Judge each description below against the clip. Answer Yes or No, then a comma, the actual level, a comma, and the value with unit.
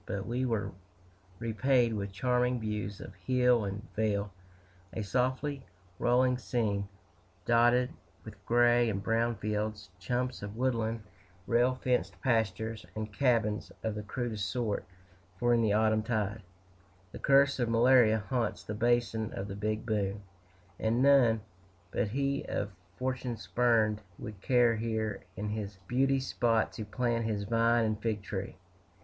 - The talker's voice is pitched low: Yes, low, 115 Hz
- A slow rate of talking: No, average, 145 wpm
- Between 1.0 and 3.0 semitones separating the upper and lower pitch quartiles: Yes, average, 2.7 semitones